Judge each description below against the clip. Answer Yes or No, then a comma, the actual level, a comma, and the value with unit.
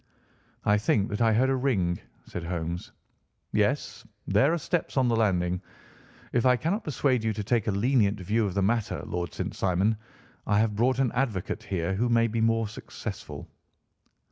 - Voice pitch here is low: Yes, low, 110 Hz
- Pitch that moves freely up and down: No, average, 4.2 semitones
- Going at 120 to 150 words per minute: No, average, 180 wpm